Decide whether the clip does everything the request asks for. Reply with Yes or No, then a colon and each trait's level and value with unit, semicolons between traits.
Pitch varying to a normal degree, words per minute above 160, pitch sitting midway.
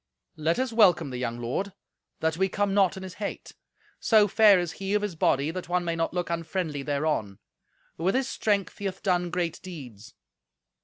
Yes: average, 3.9 semitones; average, 195 wpm; medium, 180 Hz